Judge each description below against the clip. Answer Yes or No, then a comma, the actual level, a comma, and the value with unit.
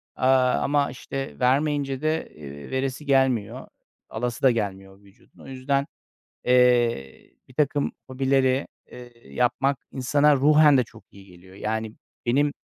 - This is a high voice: No, low, 130 Hz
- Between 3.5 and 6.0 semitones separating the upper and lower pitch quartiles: No, average, 3.1 semitones